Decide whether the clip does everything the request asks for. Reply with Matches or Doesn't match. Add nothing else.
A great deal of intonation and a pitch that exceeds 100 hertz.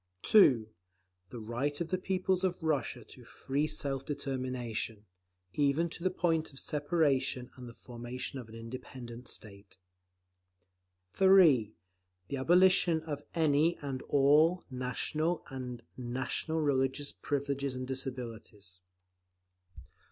Doesn't match